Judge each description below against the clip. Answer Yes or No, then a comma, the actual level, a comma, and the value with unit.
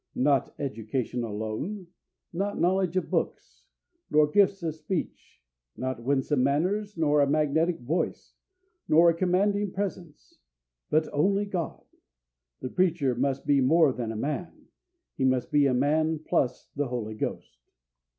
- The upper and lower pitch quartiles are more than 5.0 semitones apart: Yes, wide, 5.4 semitones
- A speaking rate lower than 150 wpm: Yes, average, 140 wpm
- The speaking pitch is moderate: Yes, medium, 150 Hz